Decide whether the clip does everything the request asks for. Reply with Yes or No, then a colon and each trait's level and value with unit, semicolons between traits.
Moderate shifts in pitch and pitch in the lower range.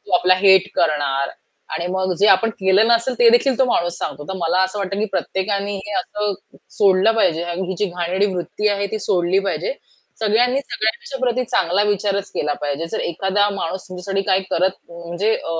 No: average, 3.2 semitones; high, 190 Hz